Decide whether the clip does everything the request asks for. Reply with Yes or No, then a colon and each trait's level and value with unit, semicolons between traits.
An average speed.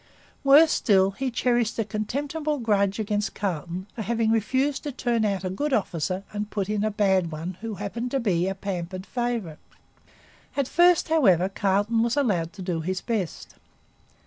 Yes: average, 170 wpm